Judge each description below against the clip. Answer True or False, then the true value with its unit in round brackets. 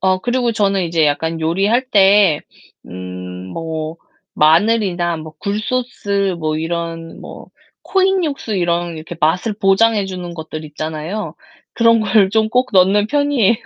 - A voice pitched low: False (190 Hz)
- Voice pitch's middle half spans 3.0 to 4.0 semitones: False (5.1 semitones)